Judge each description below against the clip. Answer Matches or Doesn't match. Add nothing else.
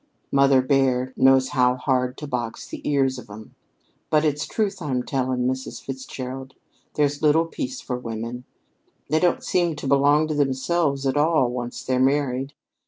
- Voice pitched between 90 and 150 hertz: Matches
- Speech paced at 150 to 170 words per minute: Matches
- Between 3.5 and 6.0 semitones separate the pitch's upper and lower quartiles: Doesn't match